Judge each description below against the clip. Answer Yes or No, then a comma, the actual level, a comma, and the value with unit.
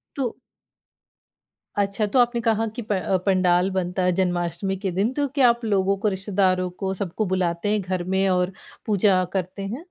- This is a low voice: No, high, 195 Hz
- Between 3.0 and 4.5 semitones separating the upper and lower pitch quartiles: No, narrow, 2.5 semitones